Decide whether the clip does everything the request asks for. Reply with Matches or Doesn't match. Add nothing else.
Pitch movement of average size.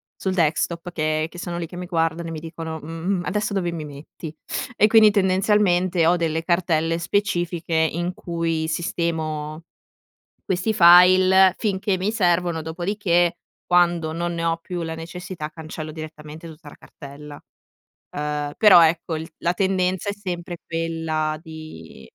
Doesn't match